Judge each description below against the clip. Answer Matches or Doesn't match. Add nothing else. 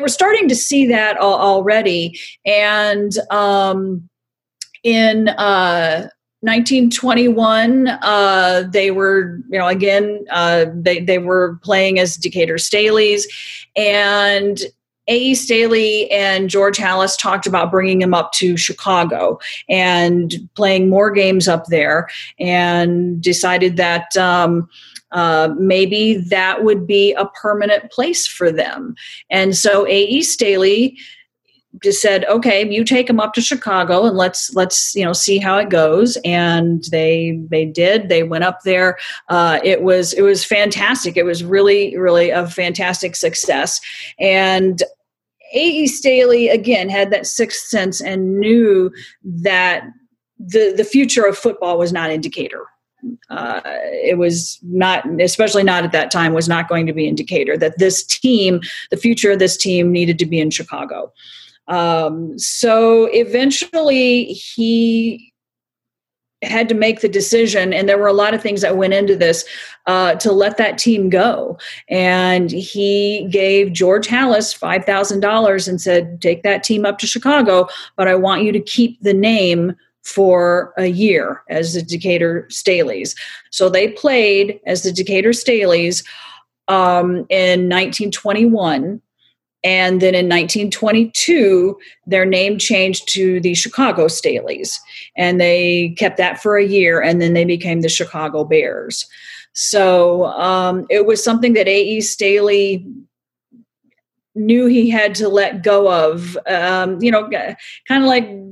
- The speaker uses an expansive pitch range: Doesn't match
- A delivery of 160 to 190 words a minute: Doesn't match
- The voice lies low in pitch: Doesn't match